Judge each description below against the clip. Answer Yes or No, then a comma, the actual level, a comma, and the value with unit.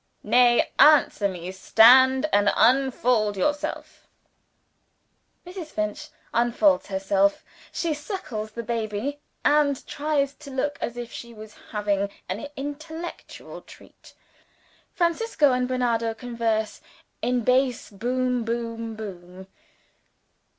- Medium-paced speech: No, slow, 105 wpm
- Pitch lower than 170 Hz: No, high, 240 Hz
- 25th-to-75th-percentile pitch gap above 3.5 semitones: Yes, average, 4.6 semitones